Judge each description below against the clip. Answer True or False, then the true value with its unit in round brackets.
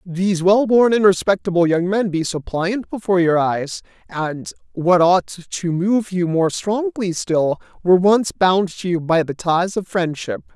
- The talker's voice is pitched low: False (185 Hz)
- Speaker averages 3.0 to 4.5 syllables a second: True (4.3 syllables/s)